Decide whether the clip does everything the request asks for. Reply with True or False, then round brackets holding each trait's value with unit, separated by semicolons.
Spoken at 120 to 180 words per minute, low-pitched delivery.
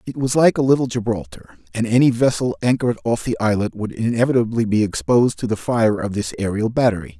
False (200 wpm; 115 Hz)